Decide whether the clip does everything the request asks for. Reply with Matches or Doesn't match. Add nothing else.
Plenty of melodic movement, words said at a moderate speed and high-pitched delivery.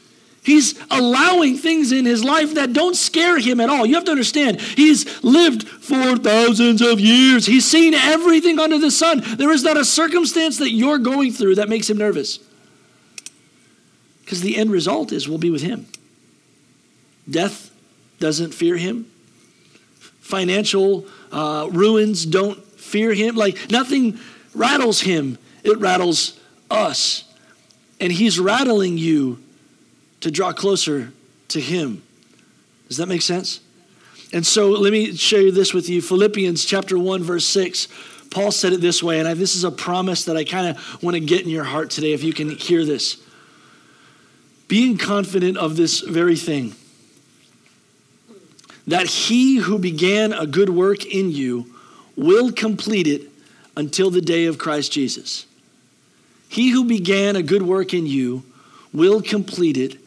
Matches